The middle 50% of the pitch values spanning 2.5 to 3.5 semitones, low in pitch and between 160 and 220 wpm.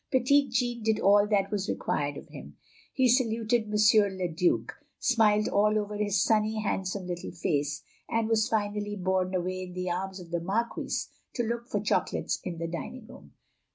No: average, 3.2 semitones; high, 210 Hz; average, 180 wpm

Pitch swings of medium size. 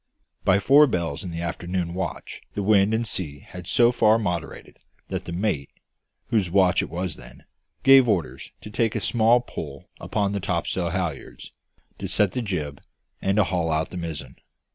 Yes: average, 4.0 semitones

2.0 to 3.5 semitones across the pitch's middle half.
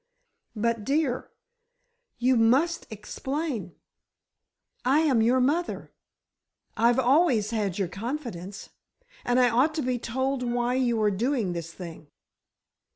No: average, 3.9 semitones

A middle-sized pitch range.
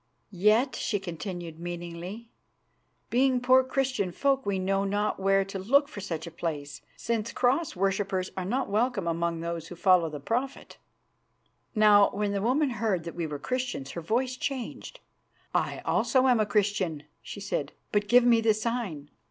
No: wide, 5.8 semitones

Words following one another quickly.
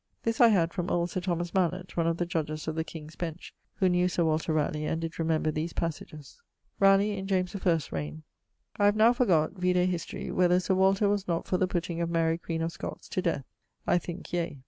Yes: fast, 225 wpm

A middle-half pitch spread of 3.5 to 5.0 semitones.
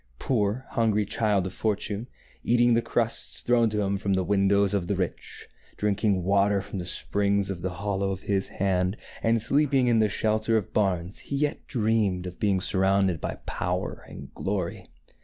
No: narrow, 2.5 semitones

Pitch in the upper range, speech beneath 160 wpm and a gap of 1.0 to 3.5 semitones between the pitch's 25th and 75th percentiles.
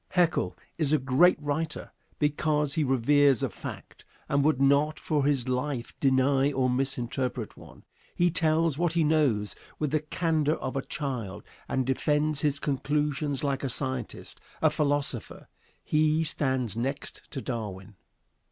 No: medium, 140 Hz; average, 145 wpm; narrow, 2.6 semitones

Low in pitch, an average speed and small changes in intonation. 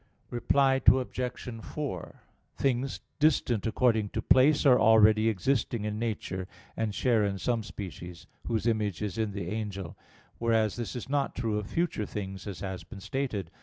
No: low, 110 Hz; average, 160 wpm; average, 3.5 semitones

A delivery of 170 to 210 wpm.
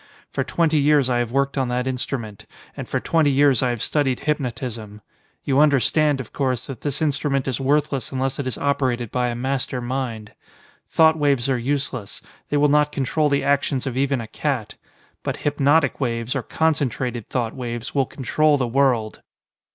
Yes: average, 180 wpm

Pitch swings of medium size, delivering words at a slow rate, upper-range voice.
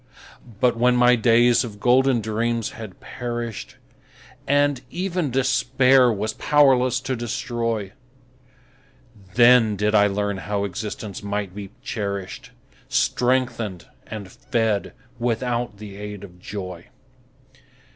No: average, 3.3 semitones; slow, 110 wpm; low, 115 Hz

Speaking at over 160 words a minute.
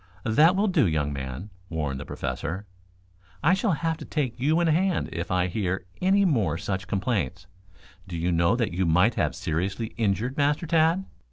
Yes: average, 180 wpm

